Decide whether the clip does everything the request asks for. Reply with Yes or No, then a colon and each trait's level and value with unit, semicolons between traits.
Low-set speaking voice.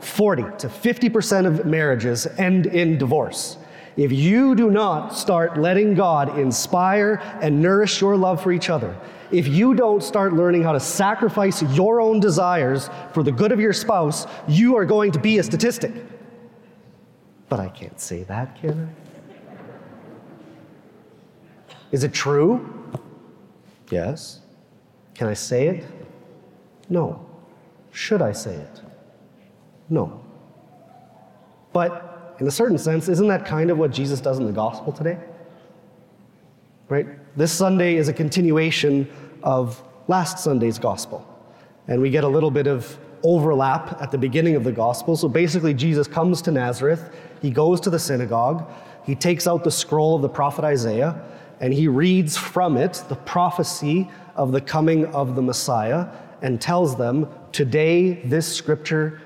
No: medium, 160 Hz